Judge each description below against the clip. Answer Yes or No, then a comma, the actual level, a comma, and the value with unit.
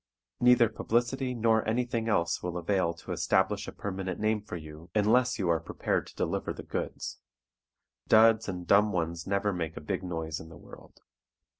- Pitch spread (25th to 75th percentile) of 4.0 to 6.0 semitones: Yes, average, 4.6 semitones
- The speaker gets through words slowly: No, average, 175 wpm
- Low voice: Yes, low, 100 Hz